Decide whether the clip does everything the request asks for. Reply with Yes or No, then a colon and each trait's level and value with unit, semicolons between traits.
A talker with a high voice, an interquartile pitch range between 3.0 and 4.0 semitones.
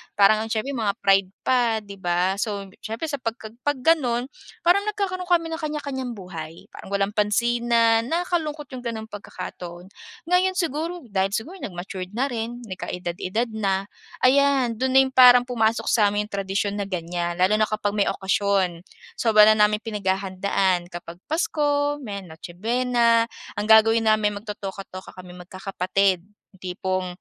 No: high, 215 Hz; average, 4.6 semitones